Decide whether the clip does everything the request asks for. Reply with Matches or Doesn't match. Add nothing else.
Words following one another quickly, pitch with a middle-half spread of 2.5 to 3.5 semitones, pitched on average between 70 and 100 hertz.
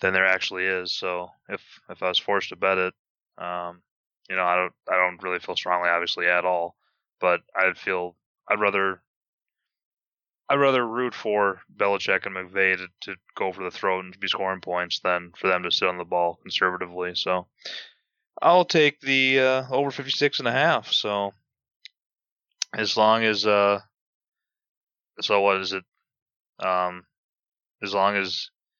Doesn't match